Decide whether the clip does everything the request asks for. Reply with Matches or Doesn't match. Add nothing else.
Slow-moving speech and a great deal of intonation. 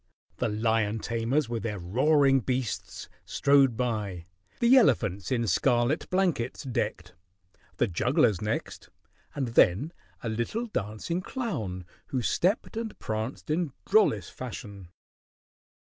Matches